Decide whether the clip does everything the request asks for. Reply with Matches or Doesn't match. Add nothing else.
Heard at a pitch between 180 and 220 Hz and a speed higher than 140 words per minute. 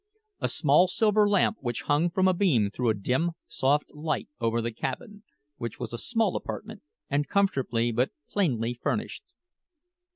Doesn't match